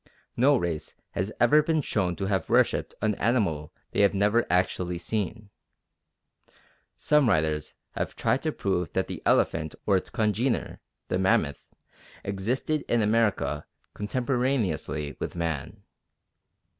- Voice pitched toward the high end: No, low, 100 Hz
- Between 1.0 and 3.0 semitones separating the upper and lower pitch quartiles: No, average, 5.3 semitones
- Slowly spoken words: Yes, slow, 130 wpm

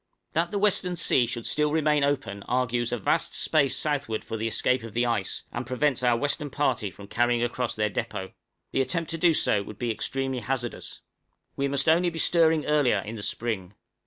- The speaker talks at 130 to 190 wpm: No, average, 200 wpm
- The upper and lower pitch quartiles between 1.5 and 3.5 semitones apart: No, average, 4.7 semitones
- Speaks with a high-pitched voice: No, low, 130 Hz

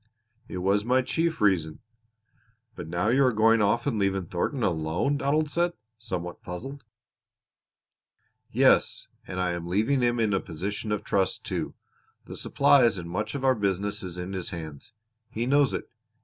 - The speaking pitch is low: Yes, low, 105 Hz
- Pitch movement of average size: No, wide, 6.0 semitones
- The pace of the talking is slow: No, average, 165 wpm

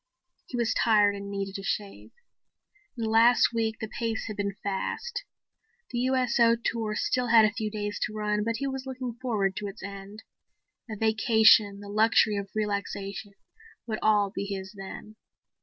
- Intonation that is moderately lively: No, narrow, 2.2 semitones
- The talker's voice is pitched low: No, high, 215 Hz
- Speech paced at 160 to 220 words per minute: Yes, average, 175 wpm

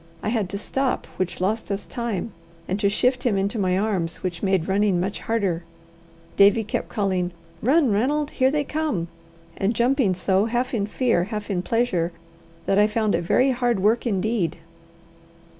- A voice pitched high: Yes, high, 210 Hz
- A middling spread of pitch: Yes, average, 4.0 semitones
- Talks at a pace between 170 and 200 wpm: Yes, average, 175 wpm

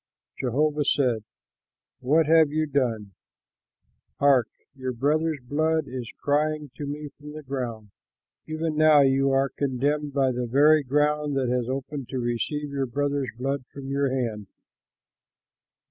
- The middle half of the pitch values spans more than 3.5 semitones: No, average, 2.7 semitones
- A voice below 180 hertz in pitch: Yes, medium, 140 Hz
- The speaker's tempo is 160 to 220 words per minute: No, average, 140 wpm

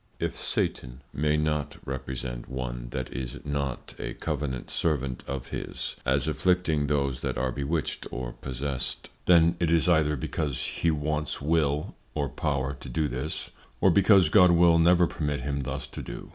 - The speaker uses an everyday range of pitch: Yes, average, 3.3 semitones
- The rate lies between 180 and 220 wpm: No, average, 170 wpm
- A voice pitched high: No, very low, 75 Hz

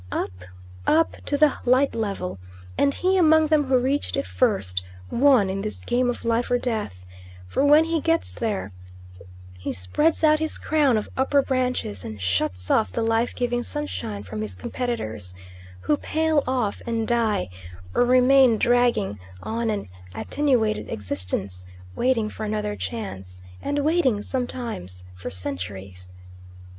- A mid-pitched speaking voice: No, high, 230 Hz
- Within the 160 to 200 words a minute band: No, average, 150 wpm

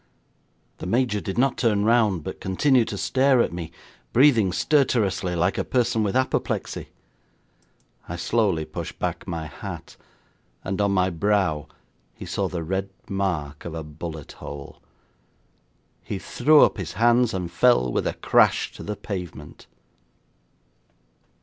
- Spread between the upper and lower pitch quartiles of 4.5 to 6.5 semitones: Yes, wide, 5.5 semitones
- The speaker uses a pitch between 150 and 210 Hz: No, very low, 95 Hz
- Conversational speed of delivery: Yes, average, 145 wpm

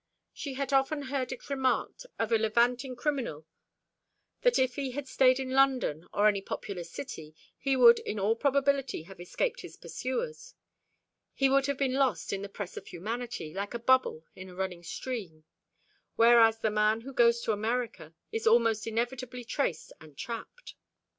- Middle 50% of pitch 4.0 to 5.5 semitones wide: Yes, average, 4.5 semitones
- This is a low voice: No, high, 235 Hz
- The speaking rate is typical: Yes, average, 170 wpm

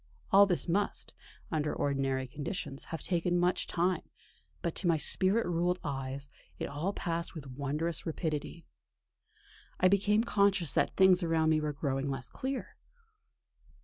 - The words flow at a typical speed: Yes, average, 145 wpm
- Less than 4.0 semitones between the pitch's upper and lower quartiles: No, average, 4.3 semitones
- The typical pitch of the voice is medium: Yes, medium, 165 Hz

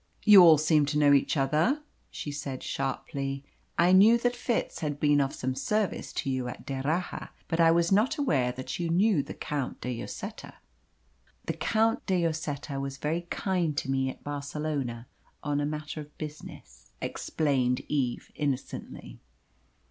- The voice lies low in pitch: No, medium, 150 Hz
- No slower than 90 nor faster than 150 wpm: No, average, 165 wpm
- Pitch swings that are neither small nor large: Yes, average, 3.9 semitones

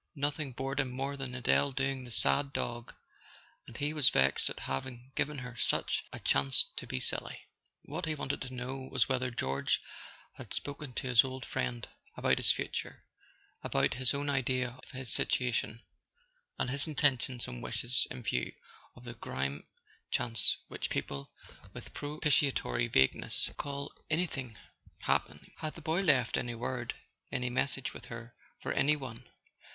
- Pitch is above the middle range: No, low, 130 Hz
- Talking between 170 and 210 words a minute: No, average, 160 wpm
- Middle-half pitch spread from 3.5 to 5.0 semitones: No, average, 2.9 semitones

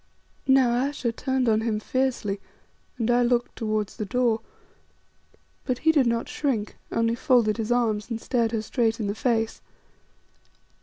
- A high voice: Yes, high, 235 Hz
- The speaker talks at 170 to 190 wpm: No, average, 155 wpm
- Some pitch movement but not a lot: No, narrow, 2.2 semitones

